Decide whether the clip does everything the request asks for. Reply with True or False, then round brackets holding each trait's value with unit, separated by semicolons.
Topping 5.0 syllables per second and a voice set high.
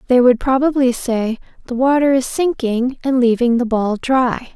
False (4.5 syllables/s; 250 Hz)